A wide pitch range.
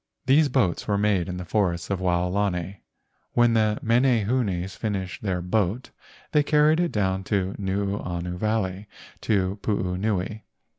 No: average, 3.2 semitones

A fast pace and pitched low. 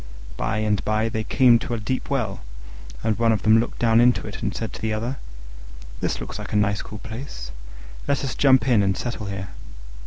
Yes: fast, 210 wpm; low, 110 Hz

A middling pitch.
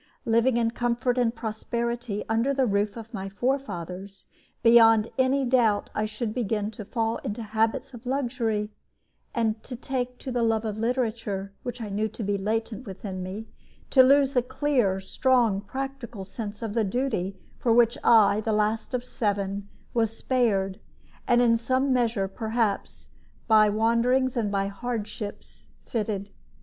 No: high, 225 Hz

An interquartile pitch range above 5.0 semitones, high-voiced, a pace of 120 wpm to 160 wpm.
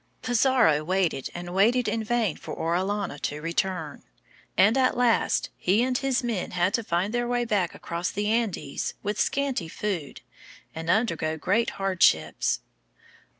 Yes: wide, 5.5 semitones; high, 200 Hz; average, 150 wpm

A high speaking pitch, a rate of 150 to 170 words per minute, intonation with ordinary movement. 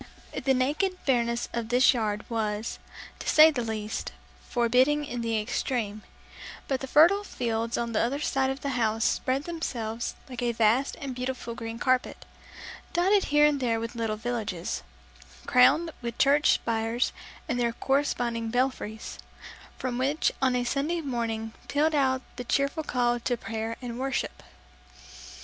Yes: high, 245 Hz; average, 155 wpm; average, 3.1 semitones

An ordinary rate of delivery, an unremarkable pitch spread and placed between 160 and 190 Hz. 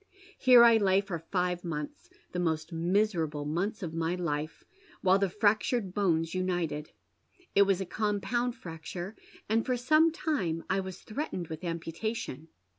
Yes: average, 165 wpm; average, 4.5 semitones; medium, 185 Hz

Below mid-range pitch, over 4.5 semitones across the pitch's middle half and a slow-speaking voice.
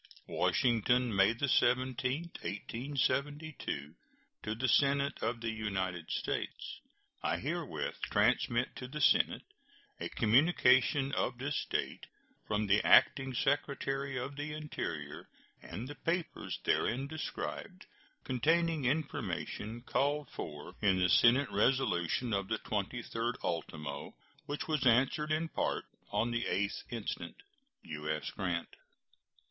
Yes: low, 125 Hz; average, 5.0 semitones; slow, 120 wpm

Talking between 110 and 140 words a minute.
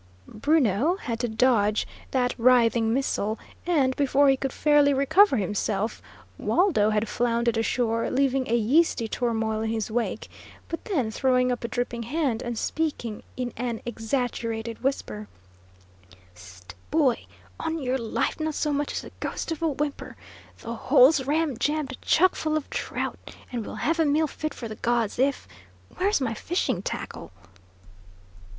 No: average, 155 wpm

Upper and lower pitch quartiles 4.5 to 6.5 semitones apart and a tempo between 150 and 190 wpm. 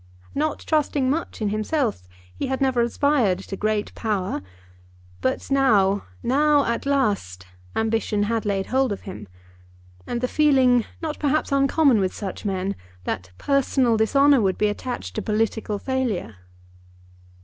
No: average, 5.2 semitones; average, 140 wpm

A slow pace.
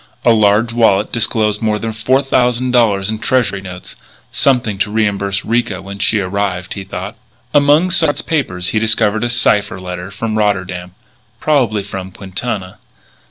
No: average, 155 wpm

